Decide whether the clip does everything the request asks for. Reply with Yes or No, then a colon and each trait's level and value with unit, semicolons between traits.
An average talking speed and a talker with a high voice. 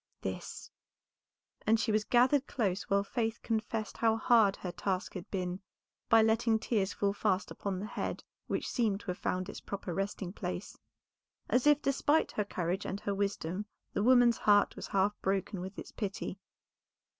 Yes: average, 170 wpm; high, 205 Hz